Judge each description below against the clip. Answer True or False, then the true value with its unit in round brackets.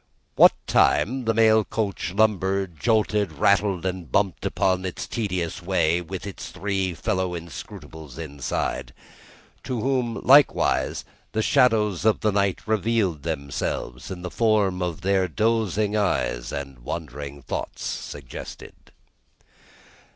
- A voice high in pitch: False (95 Hz)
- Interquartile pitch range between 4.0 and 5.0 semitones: True (4.6 semitones)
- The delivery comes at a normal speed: False (120 wpm)